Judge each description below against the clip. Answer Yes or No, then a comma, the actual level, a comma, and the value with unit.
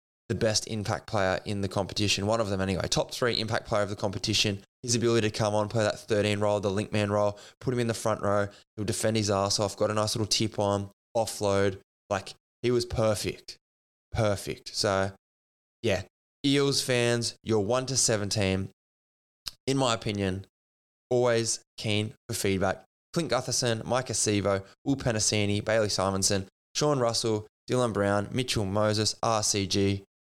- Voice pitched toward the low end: Yes, low, 105 Hz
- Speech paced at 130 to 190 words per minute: Yes, average, 165 wpm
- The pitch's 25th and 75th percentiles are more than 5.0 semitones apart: No, narrow, 2.6 semitones